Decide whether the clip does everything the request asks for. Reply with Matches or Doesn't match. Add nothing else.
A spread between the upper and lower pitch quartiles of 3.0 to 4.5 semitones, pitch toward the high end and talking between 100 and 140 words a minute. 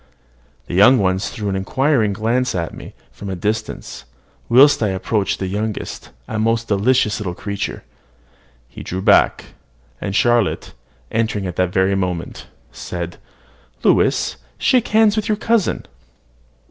Doesn't match